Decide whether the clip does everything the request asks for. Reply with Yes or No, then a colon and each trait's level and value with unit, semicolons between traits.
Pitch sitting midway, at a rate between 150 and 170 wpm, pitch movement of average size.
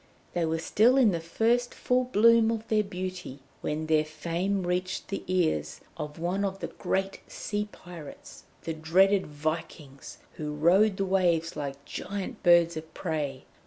Yes: medium, 175 Hz; average, 160 wpm; average, 4.1 semitones